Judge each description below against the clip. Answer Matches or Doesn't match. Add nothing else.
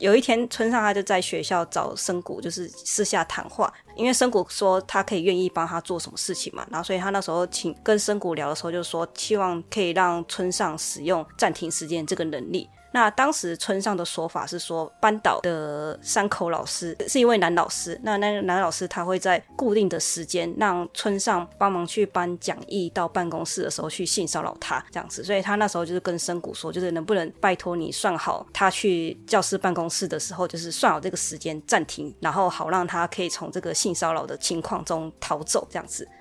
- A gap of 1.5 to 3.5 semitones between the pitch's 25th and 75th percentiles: Matches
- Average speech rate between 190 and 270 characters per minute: Doesn't match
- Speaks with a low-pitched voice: Doesn't match